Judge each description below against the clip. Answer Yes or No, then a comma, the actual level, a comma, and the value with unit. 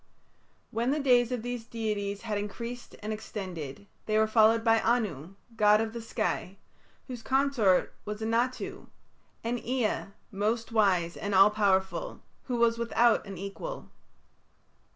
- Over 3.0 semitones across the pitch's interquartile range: No, average, 2.7 semitones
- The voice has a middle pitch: No, high, 220 Hz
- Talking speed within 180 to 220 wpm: No, average, 140 wpm